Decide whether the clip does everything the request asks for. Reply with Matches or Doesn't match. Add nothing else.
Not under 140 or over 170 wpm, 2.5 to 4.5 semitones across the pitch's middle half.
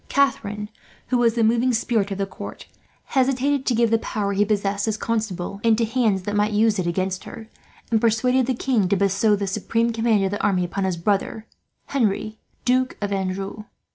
Doesn't match